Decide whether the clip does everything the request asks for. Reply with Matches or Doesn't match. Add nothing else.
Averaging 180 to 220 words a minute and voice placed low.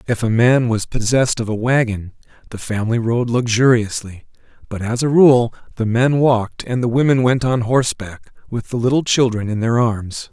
Matches